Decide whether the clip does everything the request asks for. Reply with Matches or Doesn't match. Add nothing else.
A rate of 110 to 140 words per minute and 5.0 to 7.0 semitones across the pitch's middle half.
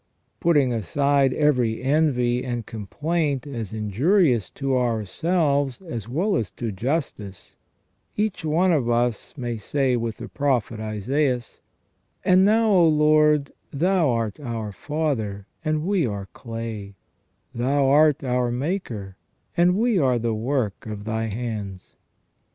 Matches